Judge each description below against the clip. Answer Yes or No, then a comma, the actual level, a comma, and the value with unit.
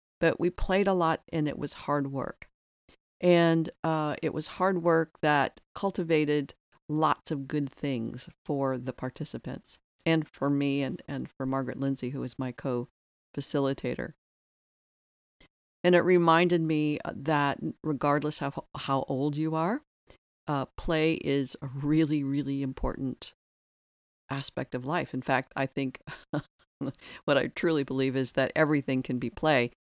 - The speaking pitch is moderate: Yes, medium, 145 Hz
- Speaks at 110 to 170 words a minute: Yes, average, 145 wpm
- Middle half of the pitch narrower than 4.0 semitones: Yes, average, 3.1 semitones